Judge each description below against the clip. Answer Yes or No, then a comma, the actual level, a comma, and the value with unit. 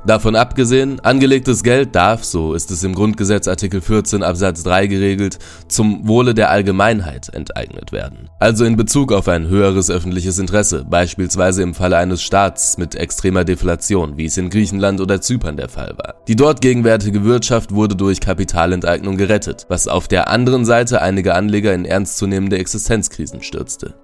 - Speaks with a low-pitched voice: Yes, low, 100 Hz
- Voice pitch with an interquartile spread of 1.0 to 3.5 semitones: Yes, average, 3.1 semitones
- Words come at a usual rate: Yes, average, 160 wpm